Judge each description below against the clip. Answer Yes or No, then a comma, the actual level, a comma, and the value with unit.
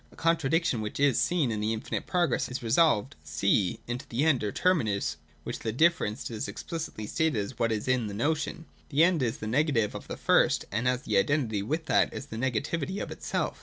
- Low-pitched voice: Yes, low, 125 Hz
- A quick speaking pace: Yes, fast, 210 wpm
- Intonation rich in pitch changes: Yes, wide, 6.4 semitones